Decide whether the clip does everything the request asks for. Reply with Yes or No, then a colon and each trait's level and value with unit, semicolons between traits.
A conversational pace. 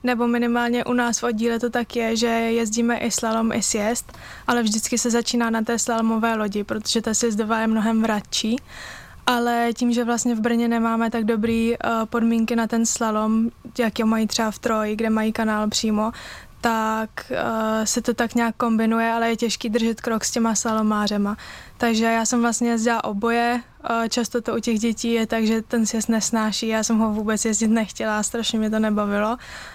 No: fast, 195 wpm